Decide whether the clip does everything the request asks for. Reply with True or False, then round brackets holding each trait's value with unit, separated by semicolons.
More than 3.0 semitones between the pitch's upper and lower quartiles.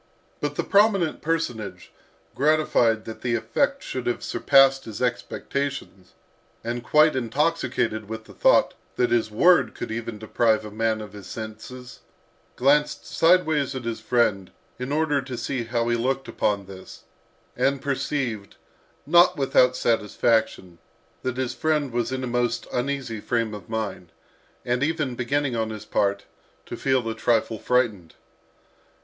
True (3.8 semitones)